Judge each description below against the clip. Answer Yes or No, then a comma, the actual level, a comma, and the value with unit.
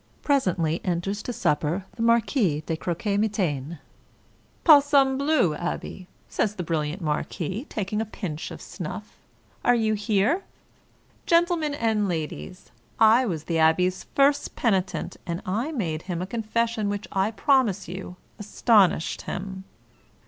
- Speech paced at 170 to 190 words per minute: No, slow, 135 wpm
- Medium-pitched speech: No, high, 200 Hz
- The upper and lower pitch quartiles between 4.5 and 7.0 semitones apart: Yes, average, 5.1 semitones